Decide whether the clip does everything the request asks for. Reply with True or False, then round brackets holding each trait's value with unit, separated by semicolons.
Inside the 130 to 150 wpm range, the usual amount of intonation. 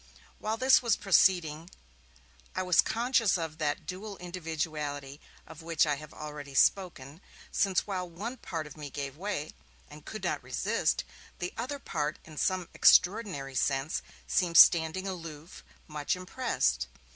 True (145 wpm; 4.1 semitones)